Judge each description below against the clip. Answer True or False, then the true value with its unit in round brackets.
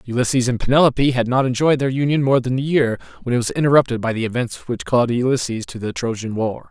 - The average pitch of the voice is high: False (125 Hz)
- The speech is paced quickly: True (235 wpm)